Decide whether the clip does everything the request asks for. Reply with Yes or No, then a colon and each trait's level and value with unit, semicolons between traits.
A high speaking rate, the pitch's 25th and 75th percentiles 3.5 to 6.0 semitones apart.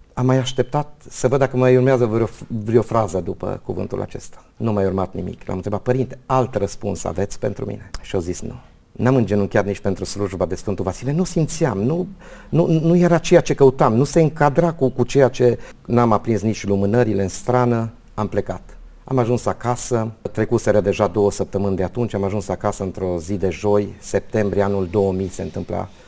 Yes: fast, 190 wpm; average, 4.4 semitones